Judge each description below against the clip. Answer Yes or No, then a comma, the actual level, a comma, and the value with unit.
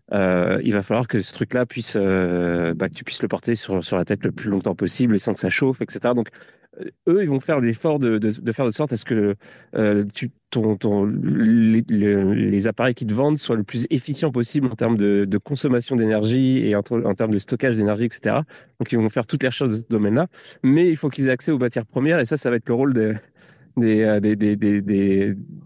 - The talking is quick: Yes, fast, 245 wpm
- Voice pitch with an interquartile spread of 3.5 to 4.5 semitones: Yes, average, 3.8 semitones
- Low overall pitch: Yes, low, 115 Hz